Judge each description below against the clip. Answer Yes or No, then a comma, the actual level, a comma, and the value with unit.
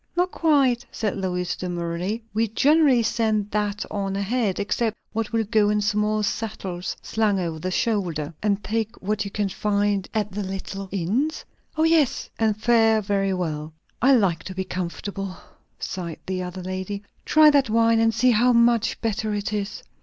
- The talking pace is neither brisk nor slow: Yes, average, 170 wpm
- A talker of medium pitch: No, high, 210 Hz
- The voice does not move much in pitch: No, average, 3.1 semitones